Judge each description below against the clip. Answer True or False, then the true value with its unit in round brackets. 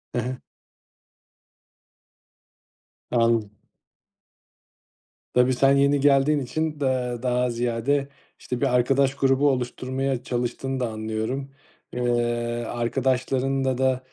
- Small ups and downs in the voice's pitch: True (2.0 semitones)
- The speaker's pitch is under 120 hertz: False (130 Hz)